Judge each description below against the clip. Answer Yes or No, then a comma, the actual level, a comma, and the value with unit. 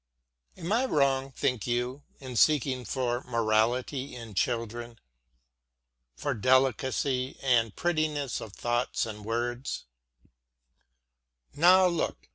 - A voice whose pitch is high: No, low, 125 Hz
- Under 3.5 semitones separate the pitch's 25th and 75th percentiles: Yes, average, 2.9 semitones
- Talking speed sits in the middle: No, slow, 100 wpm